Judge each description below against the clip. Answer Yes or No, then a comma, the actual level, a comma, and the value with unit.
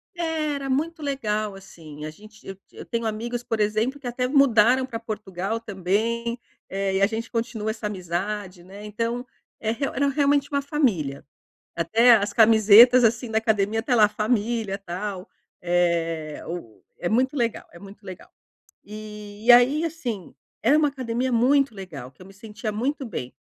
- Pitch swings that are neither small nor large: Yes, average, 4.1 semitones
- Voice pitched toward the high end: Yes, high, 220 Hz